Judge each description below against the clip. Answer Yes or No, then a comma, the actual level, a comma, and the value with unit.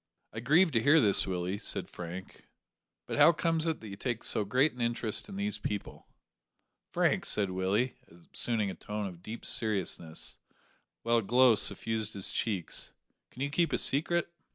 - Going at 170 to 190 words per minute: Yes, average, 175 wpm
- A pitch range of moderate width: No, wide, 6.3 semitones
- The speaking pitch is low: Yes, low, 115 Hz